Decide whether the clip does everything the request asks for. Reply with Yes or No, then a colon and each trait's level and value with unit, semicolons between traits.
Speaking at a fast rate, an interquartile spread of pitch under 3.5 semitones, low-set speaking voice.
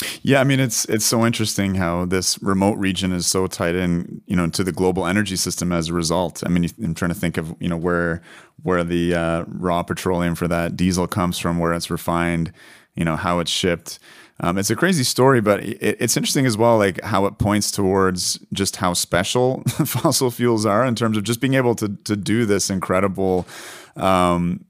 No: fast, 210 wpm; average, 4.1 semitones; very low, 95 Hz